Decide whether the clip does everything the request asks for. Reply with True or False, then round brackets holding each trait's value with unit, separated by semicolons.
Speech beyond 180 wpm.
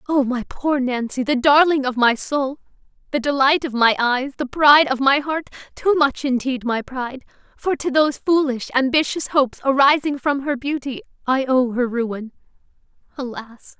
False (170 wpm)